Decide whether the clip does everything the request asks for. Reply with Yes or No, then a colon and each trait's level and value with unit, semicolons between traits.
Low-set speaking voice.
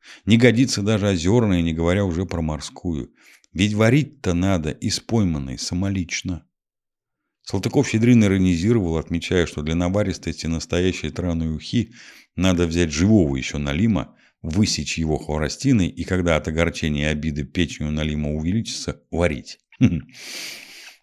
Yes: very low, 85 Hz